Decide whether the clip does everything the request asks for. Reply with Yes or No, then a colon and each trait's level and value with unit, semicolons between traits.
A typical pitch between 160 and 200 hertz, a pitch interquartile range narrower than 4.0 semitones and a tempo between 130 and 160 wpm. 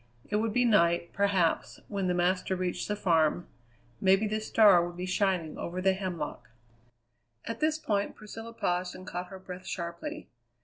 No: medium, 185 Hz; average, 2.9 semitones; average, 170 wpm